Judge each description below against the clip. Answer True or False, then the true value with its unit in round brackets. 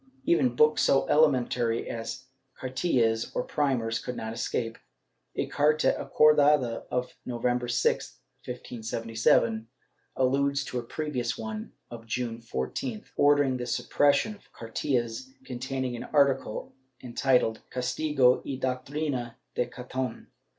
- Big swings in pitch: False (3.1 semitones)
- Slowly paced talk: True (115 wpm)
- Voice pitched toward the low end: True (125 Hz)